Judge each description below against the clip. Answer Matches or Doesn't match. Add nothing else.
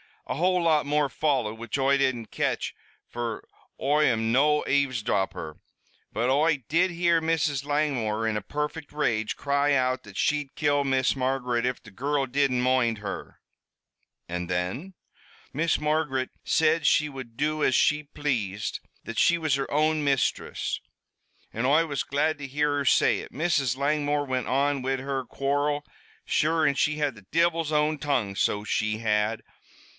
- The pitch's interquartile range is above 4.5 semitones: Doesn't match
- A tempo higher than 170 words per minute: Doesn't match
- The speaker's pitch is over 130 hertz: Matches